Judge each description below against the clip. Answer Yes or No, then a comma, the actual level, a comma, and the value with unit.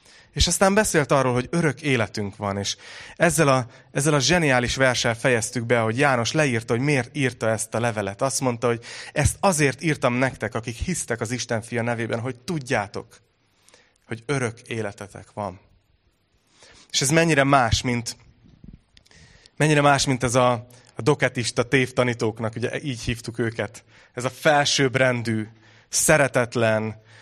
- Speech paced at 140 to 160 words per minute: Yes, average, 145 wpm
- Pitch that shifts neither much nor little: Yes, average, 3.2 semitones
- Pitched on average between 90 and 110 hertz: No, low, 125 Hz